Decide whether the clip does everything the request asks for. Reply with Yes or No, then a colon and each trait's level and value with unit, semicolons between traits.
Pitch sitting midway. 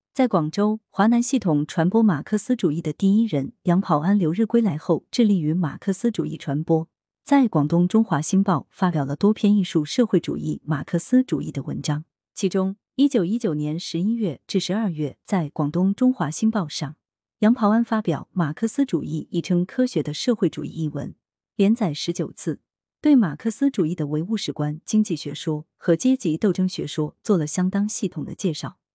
Yes: medium, 180 Hz